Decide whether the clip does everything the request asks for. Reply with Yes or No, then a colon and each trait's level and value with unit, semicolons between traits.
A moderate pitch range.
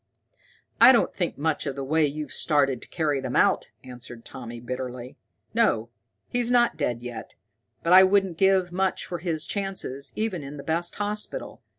No: wide, 6.5 semitones